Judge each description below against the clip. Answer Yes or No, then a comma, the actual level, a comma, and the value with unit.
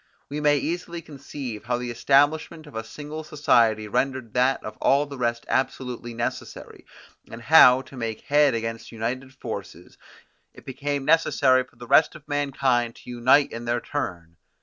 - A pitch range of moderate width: Yes, average, 3.6 semitones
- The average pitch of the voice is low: Yes, low, 130 Hz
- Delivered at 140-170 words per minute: Yes, average, 165 wpm